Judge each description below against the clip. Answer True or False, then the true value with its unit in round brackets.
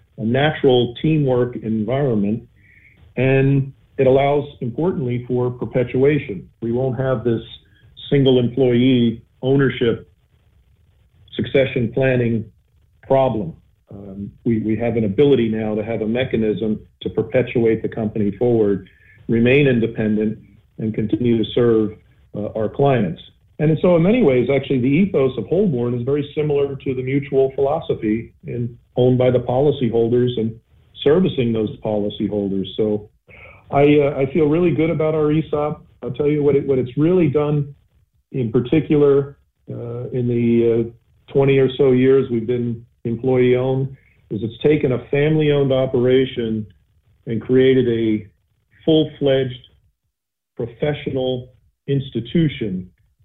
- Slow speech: True (130 wpm)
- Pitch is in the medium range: False (125 Hz)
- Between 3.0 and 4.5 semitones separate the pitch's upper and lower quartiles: True (3.8 semitones)